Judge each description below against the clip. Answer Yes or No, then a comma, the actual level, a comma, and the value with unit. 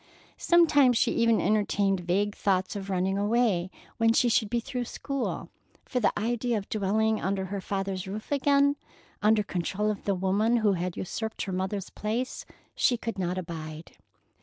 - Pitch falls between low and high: No, high, 205 Hz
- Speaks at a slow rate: No, average, 165 wpm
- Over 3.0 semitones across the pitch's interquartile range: Yes, average, 3.4 semitones